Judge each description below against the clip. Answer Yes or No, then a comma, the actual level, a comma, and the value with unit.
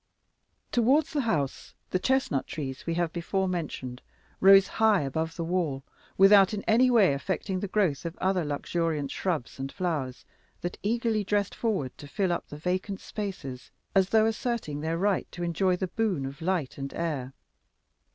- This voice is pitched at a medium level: Yes, medium, 180 Hz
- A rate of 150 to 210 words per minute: Yes, average, 170 wpm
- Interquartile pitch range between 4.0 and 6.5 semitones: Yes, wide, 5.5 semitones